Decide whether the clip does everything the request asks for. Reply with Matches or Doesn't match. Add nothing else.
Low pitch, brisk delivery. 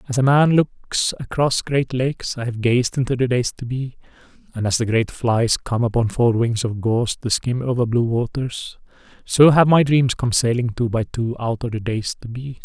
Matches